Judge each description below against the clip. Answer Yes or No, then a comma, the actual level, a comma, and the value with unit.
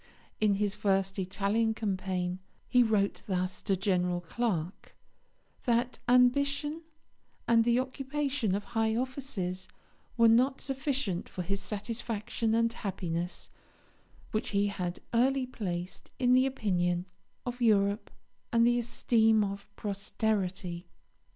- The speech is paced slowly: Yes, slow, 120 wpm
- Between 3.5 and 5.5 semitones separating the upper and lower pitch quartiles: Yes, average, 4.2 semitones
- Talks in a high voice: Yes, high, 215 Hz